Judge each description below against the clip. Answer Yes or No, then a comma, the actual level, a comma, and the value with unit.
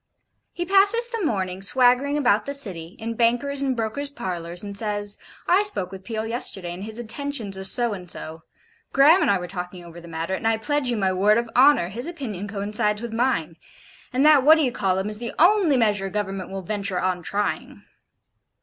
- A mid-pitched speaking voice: No, high, 215 Hz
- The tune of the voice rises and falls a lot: Yes, wide, 6.0 semitones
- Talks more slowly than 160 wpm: No, fast, 205 wpm